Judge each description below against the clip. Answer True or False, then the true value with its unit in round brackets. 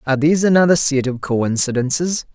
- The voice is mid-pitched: True (145 Hz)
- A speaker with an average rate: True (155 wpm)